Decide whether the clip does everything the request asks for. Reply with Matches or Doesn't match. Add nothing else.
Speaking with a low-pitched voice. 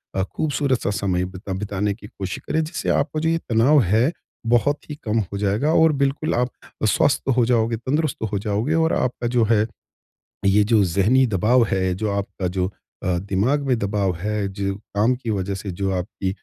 Matches